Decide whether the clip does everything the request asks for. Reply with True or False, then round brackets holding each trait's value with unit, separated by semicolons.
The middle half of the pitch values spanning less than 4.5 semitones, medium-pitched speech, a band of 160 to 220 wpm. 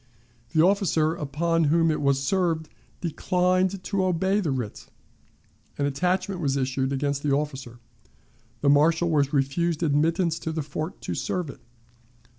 False (3.8 semitones; 160 Hz; 145 wpm)